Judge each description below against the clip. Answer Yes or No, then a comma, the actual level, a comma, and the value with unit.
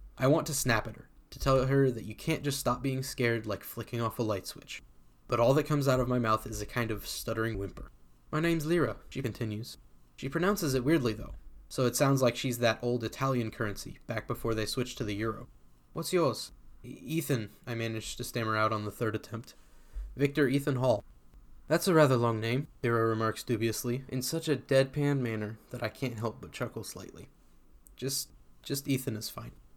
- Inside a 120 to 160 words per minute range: No, fast, 205 wpm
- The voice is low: Yes, low, 120 Hz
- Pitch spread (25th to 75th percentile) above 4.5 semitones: No, average, 3.7 semitones